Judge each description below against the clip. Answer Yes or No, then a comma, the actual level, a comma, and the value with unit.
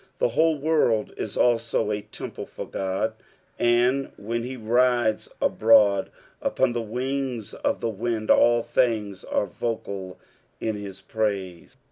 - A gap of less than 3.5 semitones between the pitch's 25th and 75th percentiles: Yes, average, 2.7 semitones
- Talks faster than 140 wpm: No, slow, 135 wpm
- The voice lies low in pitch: Yes, low, 115 Hz